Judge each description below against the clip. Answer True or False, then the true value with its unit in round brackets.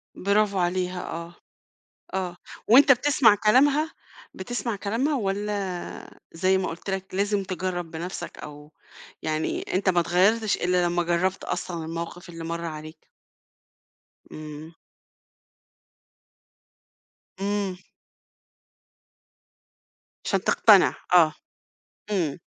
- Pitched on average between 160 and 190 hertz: True (185 Hz)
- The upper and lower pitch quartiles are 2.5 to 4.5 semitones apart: True (3.3 semitones)